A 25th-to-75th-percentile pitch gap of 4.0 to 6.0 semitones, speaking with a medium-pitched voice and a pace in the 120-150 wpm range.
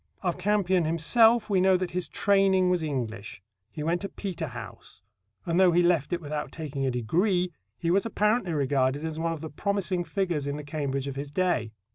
No: average, 4.5 semitones; medium, 170 Hz; average, 195 wpm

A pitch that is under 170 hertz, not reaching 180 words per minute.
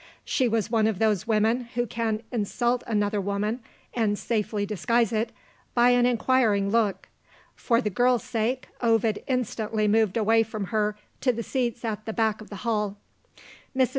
No: high, 225 Hz; average, 165 wpm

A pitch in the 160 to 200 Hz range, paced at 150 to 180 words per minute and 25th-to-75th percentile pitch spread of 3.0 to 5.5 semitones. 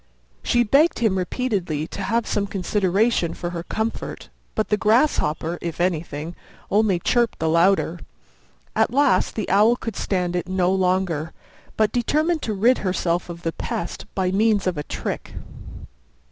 Yes: high, 190 Hz; average, 155 wpm; average, 4.2 semitones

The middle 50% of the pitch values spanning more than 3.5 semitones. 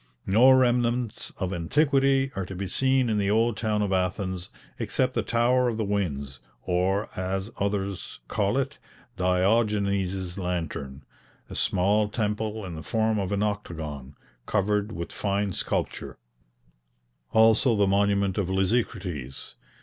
No: average, 3.2 semitones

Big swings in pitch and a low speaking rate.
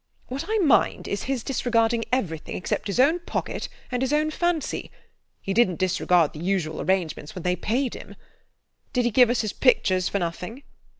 No: wide, 6.3 semitones; average, 180 wpm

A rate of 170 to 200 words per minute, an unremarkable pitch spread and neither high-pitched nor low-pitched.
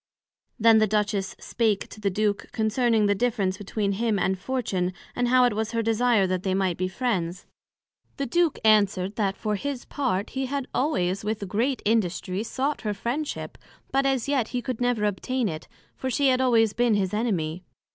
No: average, 185 wpm; average, 4.0 semitones; high, 220 Hz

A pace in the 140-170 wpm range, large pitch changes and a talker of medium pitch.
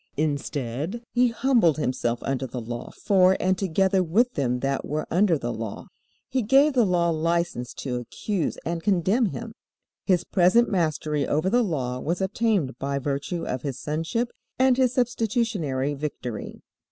Yes: average, 155 wpm; wide, 7.3 semitones; medium, 170 Hz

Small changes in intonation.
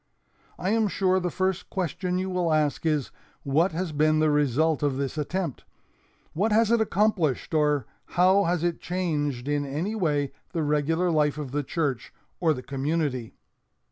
No: average, 3.8 semitones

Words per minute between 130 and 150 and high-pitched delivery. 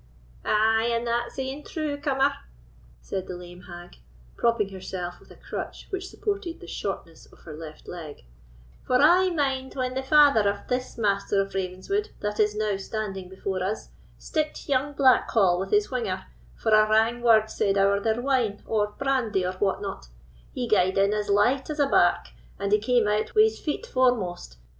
No: average, 180 wpm; high, 215 Hz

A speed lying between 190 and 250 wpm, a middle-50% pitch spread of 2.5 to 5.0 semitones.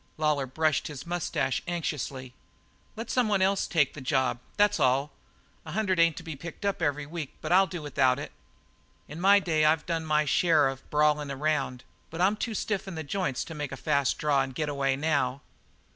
Yes: average, 195 wpm; average, 3.8 semitones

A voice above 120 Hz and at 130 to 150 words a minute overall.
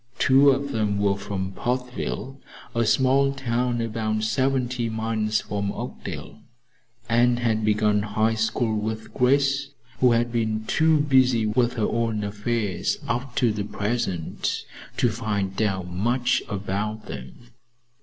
No: low, 115 Hz; slow, 135 wpm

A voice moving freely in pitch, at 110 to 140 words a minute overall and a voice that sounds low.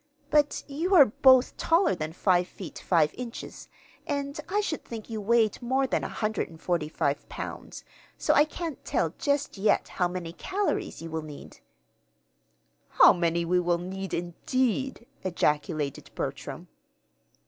No: wide, 8.0 semitones; slow, 135 wpm; high, 195 Hz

